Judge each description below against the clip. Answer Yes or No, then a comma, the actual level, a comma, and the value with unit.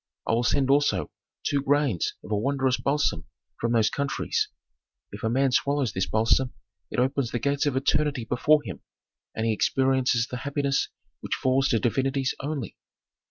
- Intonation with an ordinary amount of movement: Yes, average, 3.1 semitones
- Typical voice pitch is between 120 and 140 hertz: Yes, low, 135 Hz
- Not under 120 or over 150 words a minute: No, average, 165 wpm